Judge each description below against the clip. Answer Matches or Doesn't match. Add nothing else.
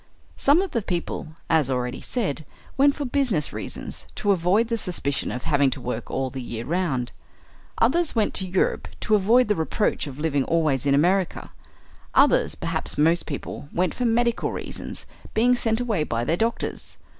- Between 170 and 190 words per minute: Matches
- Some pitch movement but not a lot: Doesn't match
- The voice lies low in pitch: Doesn't match